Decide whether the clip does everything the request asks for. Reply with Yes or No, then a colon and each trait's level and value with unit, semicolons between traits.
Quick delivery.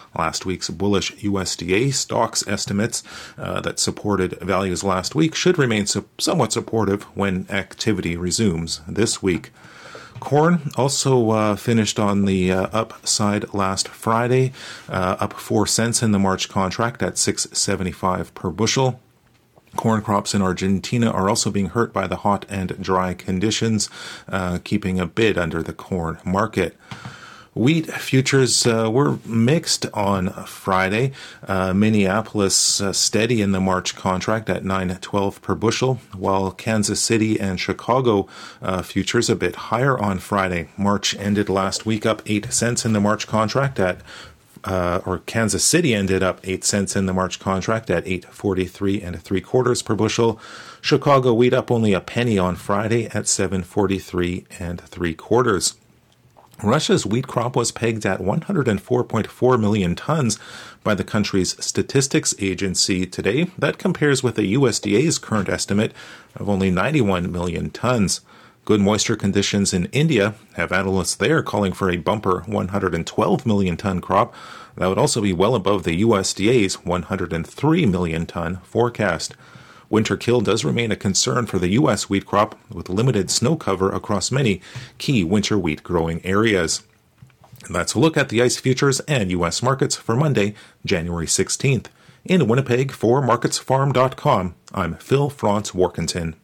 No: average, 150 wpm